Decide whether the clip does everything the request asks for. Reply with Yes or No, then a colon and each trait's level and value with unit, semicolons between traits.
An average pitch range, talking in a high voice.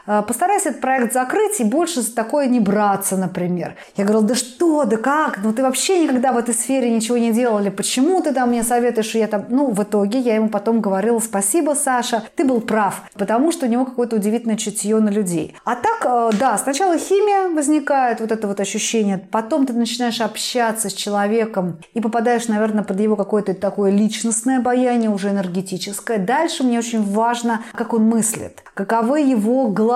Yes: average, 3.5 semitones; high, 230 Hz